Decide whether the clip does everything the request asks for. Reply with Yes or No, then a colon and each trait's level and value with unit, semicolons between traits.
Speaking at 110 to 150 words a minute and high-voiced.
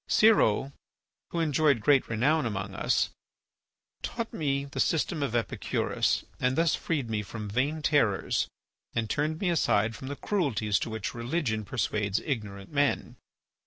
No: average, 145 wpm; low, 130 Hz